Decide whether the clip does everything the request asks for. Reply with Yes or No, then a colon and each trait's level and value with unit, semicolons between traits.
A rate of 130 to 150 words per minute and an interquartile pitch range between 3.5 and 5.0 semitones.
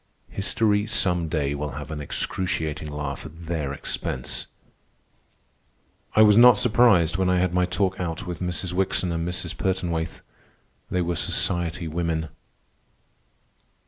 No: slow, 135 wpm; average, 2.7 semitones